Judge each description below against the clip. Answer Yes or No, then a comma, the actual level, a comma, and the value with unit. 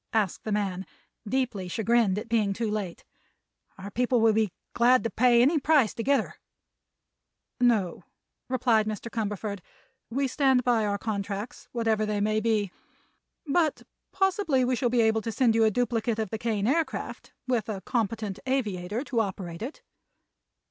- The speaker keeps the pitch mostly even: No, average, 3.1 semitones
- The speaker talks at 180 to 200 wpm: No, average, 160 wpm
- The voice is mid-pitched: No, high, 225 Hz